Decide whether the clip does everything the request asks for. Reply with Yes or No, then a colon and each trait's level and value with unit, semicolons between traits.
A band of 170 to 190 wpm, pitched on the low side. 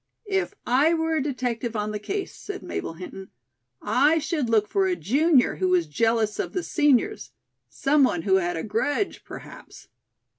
No: average, 175 wpm; very high, 255 Hz